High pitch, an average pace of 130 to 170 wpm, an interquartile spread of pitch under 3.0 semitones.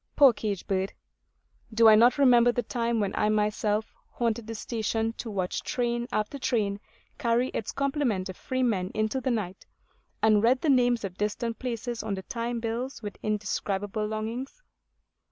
Yes: high, 225 Hz; average, 165 wpm; narrow, 2.5 semitones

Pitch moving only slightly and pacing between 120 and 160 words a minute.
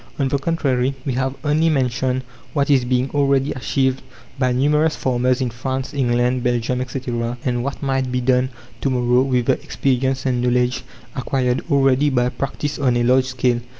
No: narrow, 1.6 semitones; average, 175 wpm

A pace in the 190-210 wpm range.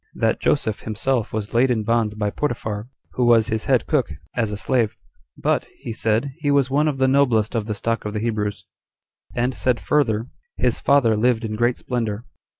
Yes: average, 195 wpm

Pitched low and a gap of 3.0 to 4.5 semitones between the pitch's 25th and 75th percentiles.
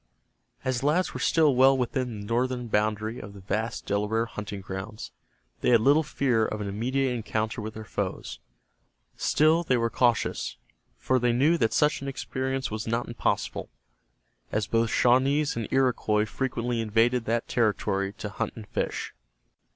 Yes: low, 115 Hz; average, 3.3 semitones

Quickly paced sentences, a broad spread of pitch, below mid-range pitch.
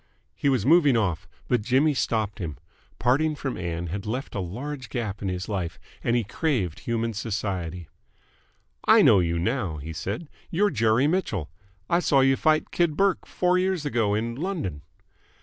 No: average, 170 wpm; wide, 7.5 semitones; low, 115 Hz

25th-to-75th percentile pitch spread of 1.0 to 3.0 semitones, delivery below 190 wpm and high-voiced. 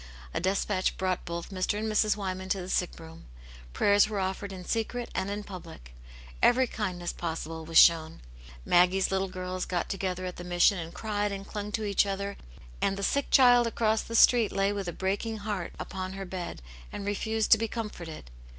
No: narrow, 2.6 semitones; average, 195 wpm; high, 195 Hz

